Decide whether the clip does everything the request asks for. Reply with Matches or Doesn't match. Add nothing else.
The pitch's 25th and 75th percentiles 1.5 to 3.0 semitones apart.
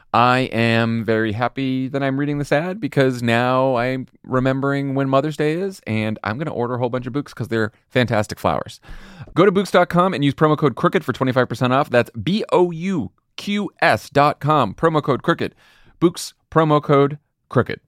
Doesn't match